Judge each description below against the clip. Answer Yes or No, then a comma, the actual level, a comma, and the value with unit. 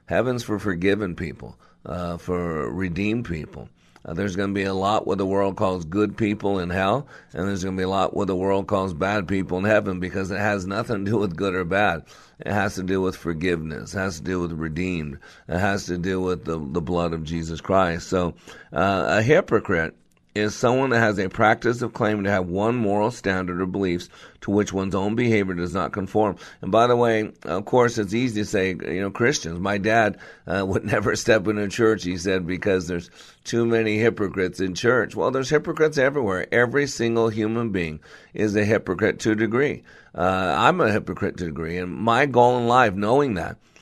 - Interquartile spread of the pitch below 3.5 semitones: Yes, average, 2.9 semitones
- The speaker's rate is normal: No, fast, 215 wpm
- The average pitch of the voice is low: Yes, low, 100 Hz